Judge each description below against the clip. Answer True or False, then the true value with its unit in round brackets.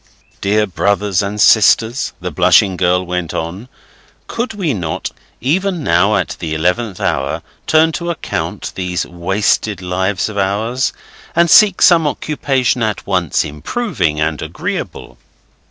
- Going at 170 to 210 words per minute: False (135 wpm)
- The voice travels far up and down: True (6.8 semitones)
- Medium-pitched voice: False (100 Hz)